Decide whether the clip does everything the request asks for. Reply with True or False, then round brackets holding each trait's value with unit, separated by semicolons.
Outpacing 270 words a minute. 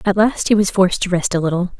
True (300 wpm)